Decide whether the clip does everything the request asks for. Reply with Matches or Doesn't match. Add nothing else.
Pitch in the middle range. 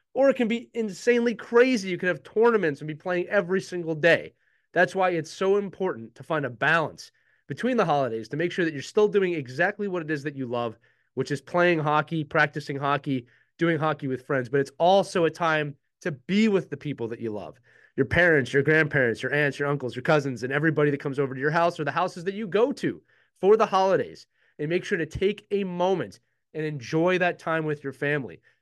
Matches